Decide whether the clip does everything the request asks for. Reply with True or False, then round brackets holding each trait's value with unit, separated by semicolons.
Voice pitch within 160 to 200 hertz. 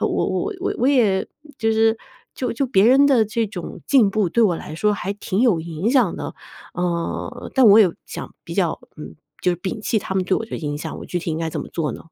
False (210 Hz)